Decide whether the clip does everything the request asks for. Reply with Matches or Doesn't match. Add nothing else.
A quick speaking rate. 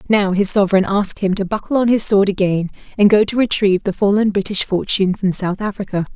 Matches